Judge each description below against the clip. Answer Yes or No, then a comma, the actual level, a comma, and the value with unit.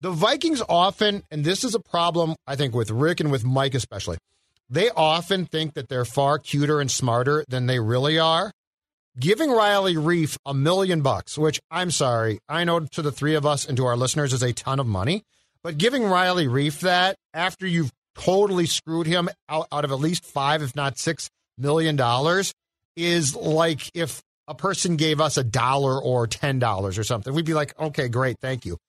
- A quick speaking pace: No, average, 195 wpm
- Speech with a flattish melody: No, average, 4.5 semitones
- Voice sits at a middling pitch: Yes, medium, 155 Hz